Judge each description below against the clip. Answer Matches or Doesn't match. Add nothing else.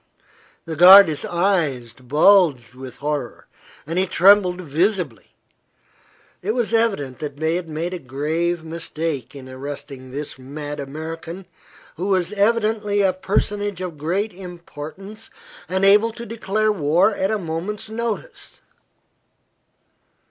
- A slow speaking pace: Matches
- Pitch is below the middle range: Doesn't match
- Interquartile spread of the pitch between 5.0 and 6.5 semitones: Matches